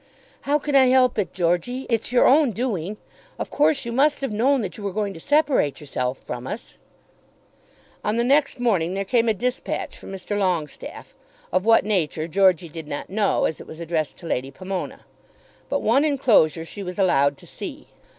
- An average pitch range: No, wide, 6.9 semitones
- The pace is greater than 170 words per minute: Yes, average, 190 wpm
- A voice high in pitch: Yes, high, 205 Hz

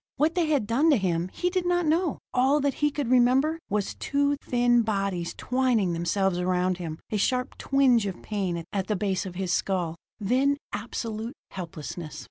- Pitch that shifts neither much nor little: No, wide, 6.9 semitones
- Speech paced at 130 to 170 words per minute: No, average, 180 wpm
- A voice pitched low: No, high, 220 Hz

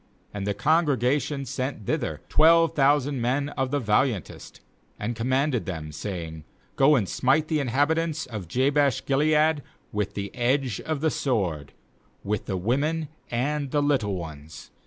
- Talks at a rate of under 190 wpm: Yes, average, 150 wpm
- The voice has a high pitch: No, low, 130 Hz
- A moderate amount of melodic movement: No, wide, 5.8 semitones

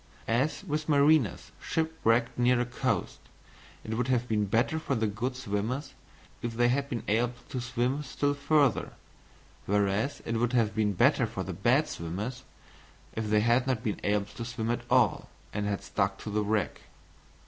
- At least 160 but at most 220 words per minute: Yes, average, 175 wpm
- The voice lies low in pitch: Yes, low, 120 Hz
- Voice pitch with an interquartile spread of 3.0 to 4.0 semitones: Yes, average, 3.4 semitones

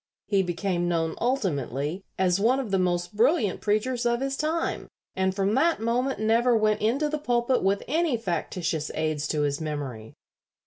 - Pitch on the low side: No, high, 205 Hz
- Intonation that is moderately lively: No, wide, 6.2 semitones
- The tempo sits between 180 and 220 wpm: No, average, 170 wpm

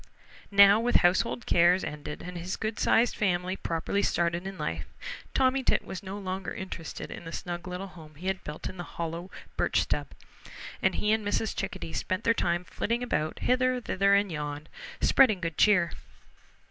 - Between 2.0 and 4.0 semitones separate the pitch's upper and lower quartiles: Yes, average, 3.4 semitones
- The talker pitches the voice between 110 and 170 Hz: No, medium, 185 Hz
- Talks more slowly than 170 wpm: No, average, 180 wpm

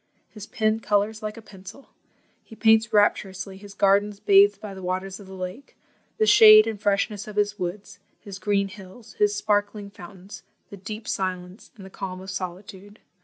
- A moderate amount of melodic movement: No, narrow, 1.9 semitones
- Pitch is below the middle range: No, high, 205 Hz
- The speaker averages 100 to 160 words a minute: No, average, 175 wpm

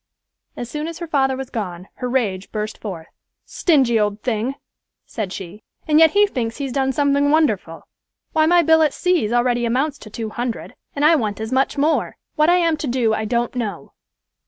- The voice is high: Yes, very high, 255 Hz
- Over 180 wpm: Yes, average, 200 wpm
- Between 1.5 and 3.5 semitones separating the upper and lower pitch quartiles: No, wide, 5.6 semitones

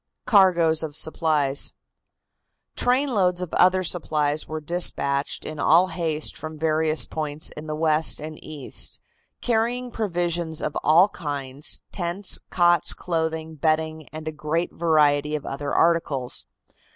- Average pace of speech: No, slow, 125 wpm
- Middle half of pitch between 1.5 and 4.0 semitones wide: Yes, narrow, 2.4 semitones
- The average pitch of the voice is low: No, medium, 160 Hz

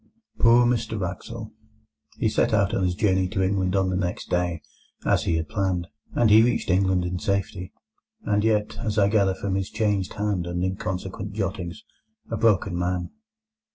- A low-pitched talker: Yes, very low, 95 Hz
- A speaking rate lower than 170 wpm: No, average, 175 wpm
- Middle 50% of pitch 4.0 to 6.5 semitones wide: No, narrow, 2.5 semitones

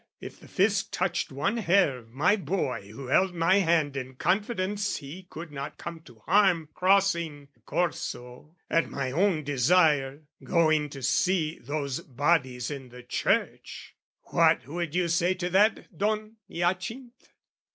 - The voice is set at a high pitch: No, medium, 165 Hz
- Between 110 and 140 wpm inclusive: No, average, 150 wpm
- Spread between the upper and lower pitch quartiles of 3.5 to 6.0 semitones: Yes, average, 5.1 semitones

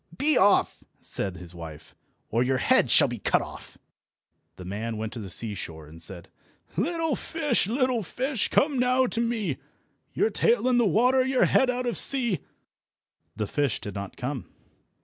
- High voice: Yes, high, 205 Hz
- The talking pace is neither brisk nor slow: Yes, average, 170 wpm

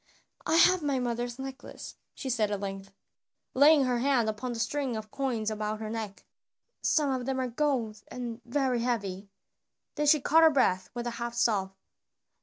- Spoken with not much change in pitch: No, average, 3.8 semitones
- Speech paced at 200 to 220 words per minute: No, average, 185 wpm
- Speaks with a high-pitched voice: Yes, high, 240 Hz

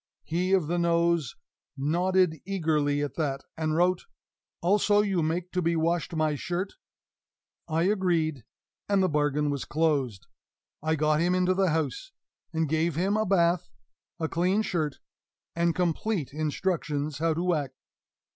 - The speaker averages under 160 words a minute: Yes, average, 145 wpm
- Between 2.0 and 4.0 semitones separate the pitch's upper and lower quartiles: Yes, average, 2.9 semitones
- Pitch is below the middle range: No, medium, 165 Hz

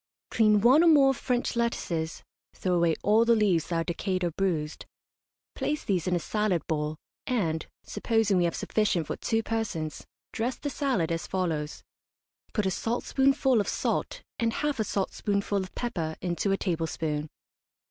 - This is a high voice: Yes, high, 195 Hz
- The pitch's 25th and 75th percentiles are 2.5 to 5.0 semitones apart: No, wide, 5.6 semitones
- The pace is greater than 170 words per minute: No, average, 165 wpm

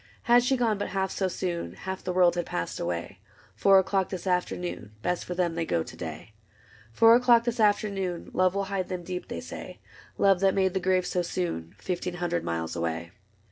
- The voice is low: No, medium, 185 Hz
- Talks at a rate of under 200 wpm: No, fast, 205 wpm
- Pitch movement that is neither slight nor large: No, narrow, 2.2 semitones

